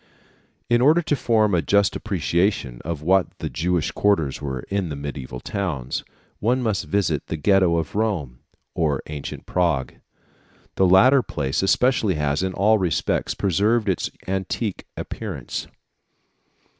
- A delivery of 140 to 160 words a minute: Yes, average, 145 wpm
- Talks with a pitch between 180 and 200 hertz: No, very low, 95 Hz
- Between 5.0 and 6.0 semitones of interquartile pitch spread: Yes, wide, 5.6 semitones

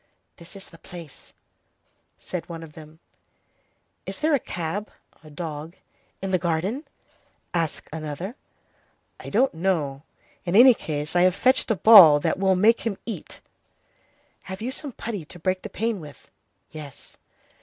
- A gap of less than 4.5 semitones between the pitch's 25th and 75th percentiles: No, average, 4.9 semitones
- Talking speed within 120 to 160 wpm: Yes, average, 150 wpm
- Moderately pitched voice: Yes, medium, 180 Hz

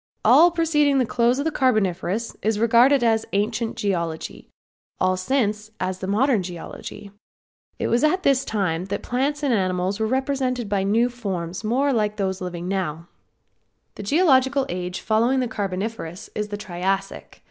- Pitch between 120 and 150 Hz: No, high, 215 Hz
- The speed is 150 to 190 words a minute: Yes, average, 160 wpm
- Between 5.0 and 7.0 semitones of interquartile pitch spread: Yes, average, 5.3 semitones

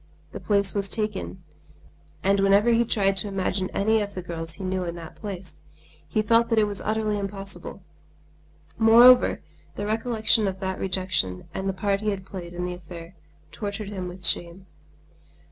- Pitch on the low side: No, high, 195 Hz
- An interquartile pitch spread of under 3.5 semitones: Yes, narrow, 2.4 semitones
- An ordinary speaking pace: Yes, average, 175 wpm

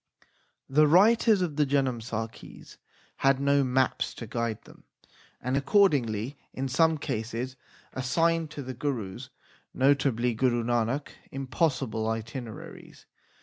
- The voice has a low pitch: Yes, low, 130 Hz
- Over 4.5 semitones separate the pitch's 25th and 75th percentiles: No, average, 3.6 semitones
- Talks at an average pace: No, slow, 110 wpm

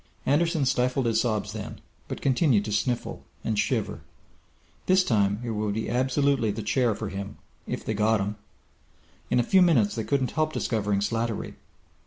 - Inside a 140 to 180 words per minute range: Yes, average, 170 wpm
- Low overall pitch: Yes, low, 115 Hz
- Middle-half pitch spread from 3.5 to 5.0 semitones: Yes, average, 4.0 semitones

